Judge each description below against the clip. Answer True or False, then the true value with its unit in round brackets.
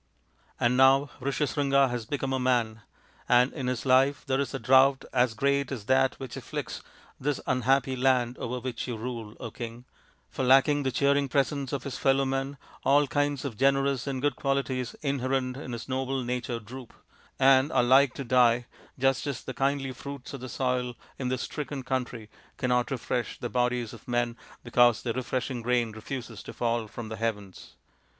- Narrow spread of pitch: True (2.0 semitones)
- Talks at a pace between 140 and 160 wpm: False (180 wpm)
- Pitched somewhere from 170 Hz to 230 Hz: False (130 Hz)